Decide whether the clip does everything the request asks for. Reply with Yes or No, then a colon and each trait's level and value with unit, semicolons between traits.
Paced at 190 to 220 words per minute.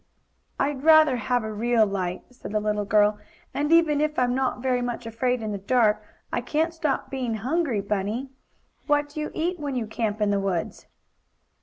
Yes: average, 195 wpm